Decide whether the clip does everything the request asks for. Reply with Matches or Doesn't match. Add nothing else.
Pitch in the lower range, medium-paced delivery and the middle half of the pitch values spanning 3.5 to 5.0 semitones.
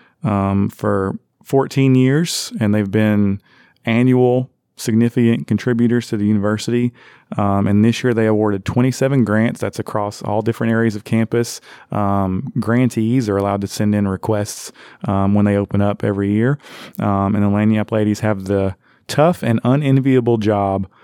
Doesn't match